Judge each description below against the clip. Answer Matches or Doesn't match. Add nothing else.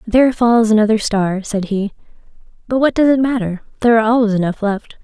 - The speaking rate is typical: Matches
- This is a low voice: Doesn't match